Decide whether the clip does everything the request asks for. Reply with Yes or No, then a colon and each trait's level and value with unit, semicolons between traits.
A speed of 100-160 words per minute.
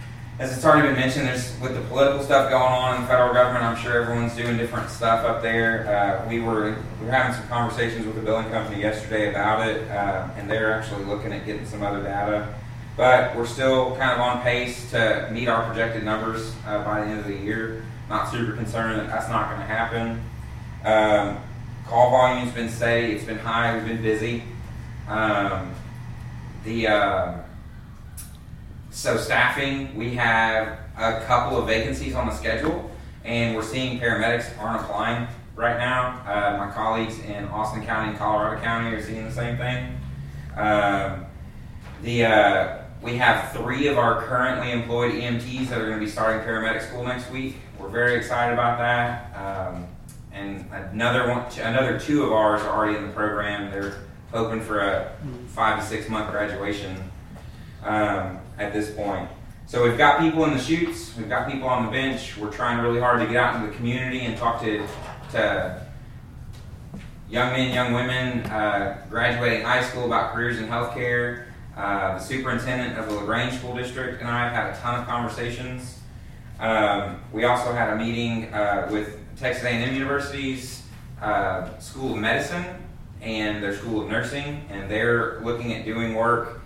No: average, 180 wpm